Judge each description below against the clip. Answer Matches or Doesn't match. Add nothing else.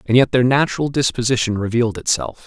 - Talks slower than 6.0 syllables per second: Doesn't match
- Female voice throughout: Doesn't match